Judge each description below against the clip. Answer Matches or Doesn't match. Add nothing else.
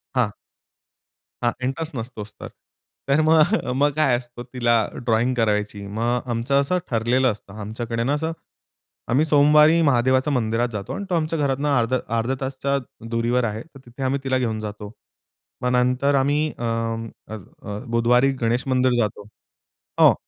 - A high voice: Doesn't match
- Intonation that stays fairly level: Doesn't match